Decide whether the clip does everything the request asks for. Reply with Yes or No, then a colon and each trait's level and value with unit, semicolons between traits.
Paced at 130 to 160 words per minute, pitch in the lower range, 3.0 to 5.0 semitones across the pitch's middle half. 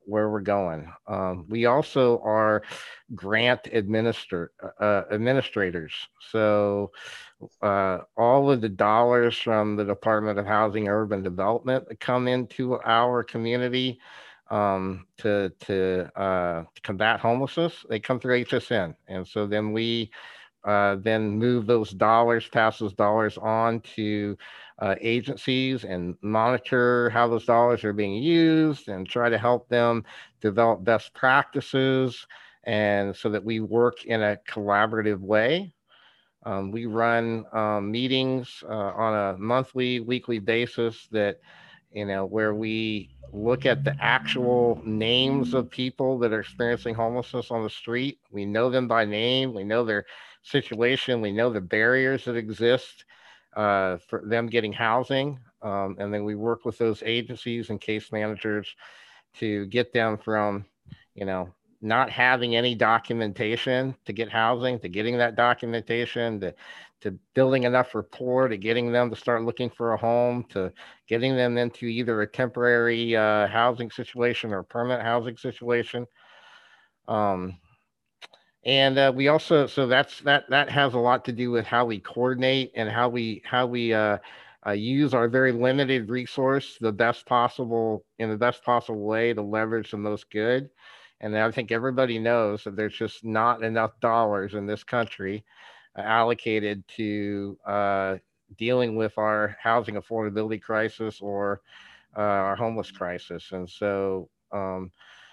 No: average, 150 wpm; low, 115 Hz; narrow, 2.6 semitones